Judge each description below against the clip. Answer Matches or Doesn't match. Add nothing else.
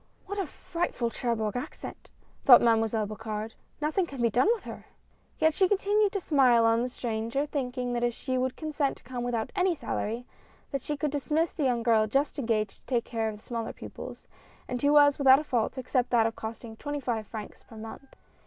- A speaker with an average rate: Doesn't match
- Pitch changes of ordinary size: Matches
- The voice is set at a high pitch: Matches